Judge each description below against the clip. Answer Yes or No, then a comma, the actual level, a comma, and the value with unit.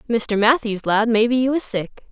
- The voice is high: Yes, high, 230 Hz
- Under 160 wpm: No, average, 200 wpm